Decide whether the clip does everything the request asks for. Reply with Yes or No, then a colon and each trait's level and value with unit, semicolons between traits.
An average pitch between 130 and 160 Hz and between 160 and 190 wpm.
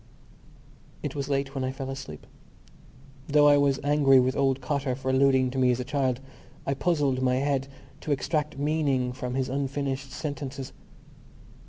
Yes: low, 135 Hz; average, 165 wpm